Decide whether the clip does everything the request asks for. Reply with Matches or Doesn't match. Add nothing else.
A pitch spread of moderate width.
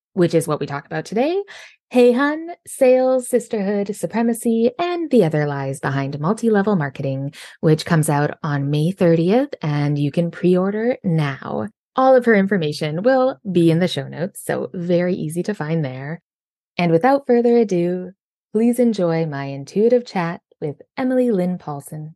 Doesn't match